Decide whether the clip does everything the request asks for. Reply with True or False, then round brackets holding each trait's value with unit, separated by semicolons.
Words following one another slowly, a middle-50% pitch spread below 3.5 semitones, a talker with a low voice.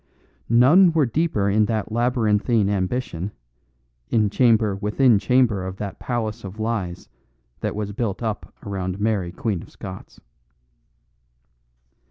True (125 wpm; 3.1 semitones; 105 Hz)